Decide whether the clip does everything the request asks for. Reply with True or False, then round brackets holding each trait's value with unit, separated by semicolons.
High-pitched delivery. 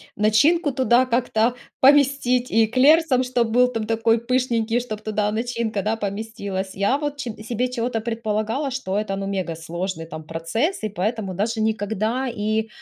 True (225 Hz)